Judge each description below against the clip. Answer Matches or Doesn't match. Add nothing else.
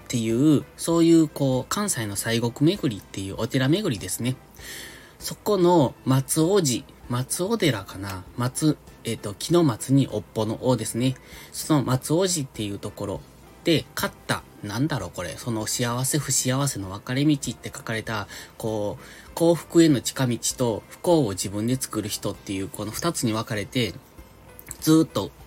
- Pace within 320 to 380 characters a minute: Doesn't match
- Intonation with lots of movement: Matches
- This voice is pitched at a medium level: Doesn't match